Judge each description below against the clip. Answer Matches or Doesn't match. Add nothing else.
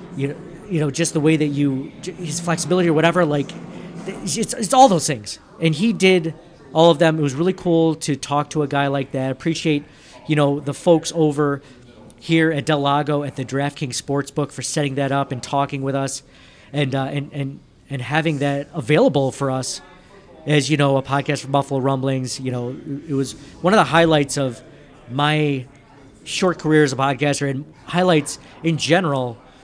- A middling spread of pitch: Matches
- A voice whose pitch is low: Doesn't match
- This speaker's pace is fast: Doesn't match